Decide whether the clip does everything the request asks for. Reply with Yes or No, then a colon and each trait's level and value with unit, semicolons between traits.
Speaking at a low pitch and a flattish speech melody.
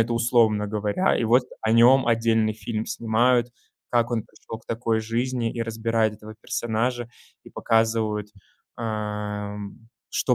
Yes: low, 115 Hz; narrow, 1.5 semitones